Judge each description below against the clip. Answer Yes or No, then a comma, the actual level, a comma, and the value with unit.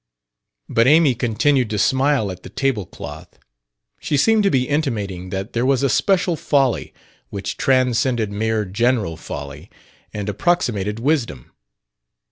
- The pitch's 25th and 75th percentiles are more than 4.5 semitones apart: Yes, average, 5.1 semitones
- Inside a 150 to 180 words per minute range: No, slow, 135 wpm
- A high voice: No, low, 120 Hz